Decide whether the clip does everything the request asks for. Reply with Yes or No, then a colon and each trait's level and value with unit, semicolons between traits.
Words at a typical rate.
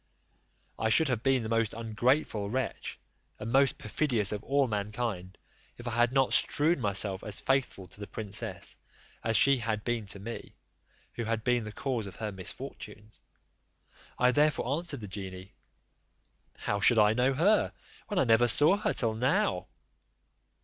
Yes: average, 165 wpm